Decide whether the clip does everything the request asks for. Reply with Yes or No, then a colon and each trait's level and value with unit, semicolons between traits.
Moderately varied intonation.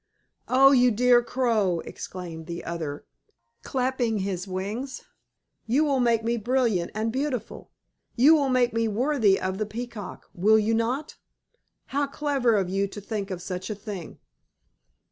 Yes: average, 4.8 semitones